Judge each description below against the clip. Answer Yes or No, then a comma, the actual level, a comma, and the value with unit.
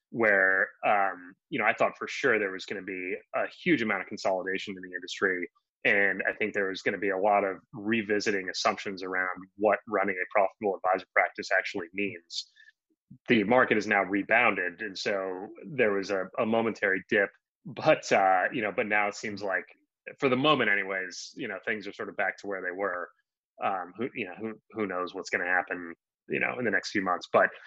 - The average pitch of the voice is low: Yes, low, 100 Hz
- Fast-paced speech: Yes, fast, 215 wpm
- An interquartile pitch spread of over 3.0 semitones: No, narrow, 2.5 semitones